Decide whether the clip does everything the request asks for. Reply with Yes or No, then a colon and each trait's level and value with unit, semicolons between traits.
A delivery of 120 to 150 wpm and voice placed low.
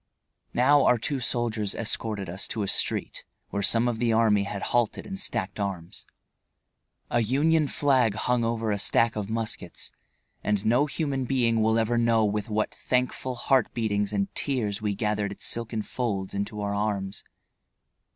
No: average, 165 wpm; low, 110 Hz